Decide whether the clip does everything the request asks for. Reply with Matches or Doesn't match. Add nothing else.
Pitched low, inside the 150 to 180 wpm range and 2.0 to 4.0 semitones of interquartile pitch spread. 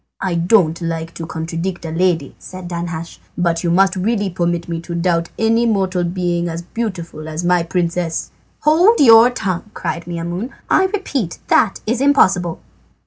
Doesn't match